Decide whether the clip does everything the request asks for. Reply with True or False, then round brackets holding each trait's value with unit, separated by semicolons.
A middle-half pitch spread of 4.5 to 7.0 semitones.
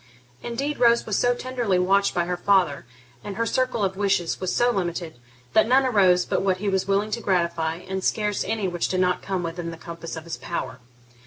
False (3.9 semitones)